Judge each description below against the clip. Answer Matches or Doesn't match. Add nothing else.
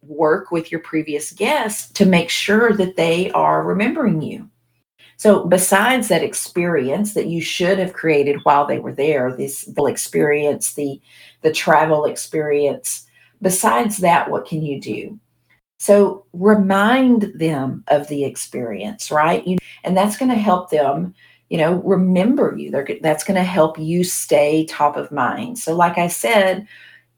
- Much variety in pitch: Doesn't match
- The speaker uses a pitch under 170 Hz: Doesn't match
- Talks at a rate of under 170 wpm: Matches